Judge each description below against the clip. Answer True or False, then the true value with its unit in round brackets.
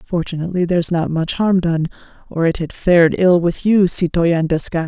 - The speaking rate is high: False (185 wpm)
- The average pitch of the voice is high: False (170 Hz)